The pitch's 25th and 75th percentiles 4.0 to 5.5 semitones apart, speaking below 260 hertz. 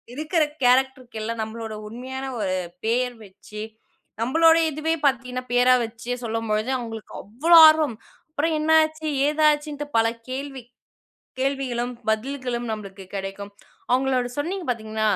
Yes: average, 4.5 semitones; very high, 250 Hz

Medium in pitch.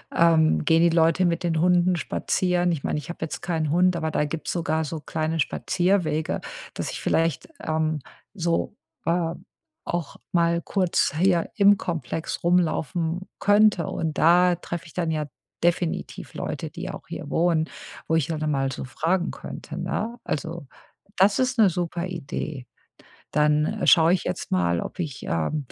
Yes: medium, 165 Hz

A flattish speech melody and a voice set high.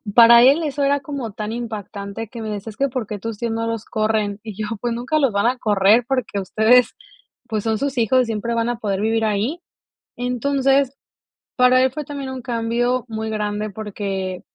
No: average, 3.1 semitones; high, 230 Hz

